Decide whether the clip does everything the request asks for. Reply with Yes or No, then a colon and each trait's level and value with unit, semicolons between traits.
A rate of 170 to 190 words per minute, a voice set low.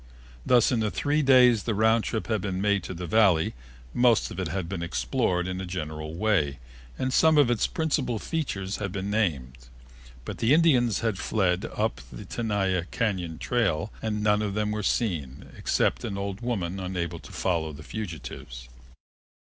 Yes: average, 175 wpm; low, 100 Hz